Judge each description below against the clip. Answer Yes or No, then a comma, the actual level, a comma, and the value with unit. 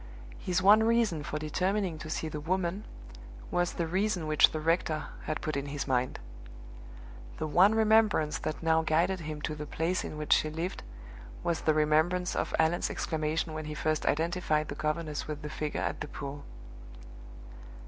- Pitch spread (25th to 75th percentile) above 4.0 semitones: No, average, 2.8 semitones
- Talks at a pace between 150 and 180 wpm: Yes, average, 175 wpm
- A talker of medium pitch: Yes, medium, 160 Hz